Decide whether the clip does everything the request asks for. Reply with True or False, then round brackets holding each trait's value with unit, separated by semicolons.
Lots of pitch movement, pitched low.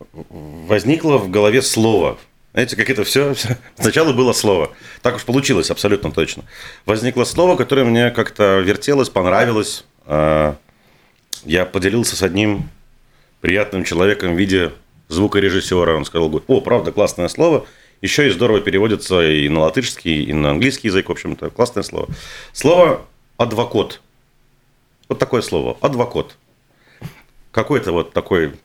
True (7.0 semitones; 100 Hz)